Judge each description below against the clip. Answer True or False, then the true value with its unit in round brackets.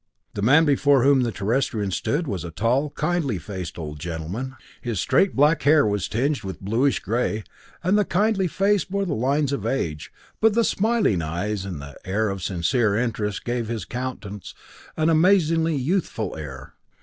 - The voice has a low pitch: True (120 Hz)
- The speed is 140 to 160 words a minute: False (175 wpm)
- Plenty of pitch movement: True (7.9 semitones)